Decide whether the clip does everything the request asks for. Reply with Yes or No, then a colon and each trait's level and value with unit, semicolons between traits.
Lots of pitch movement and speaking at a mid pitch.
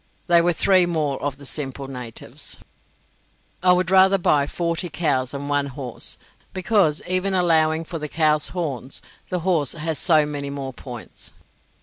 No: average, 3.9 semitones; medium, 155 Hz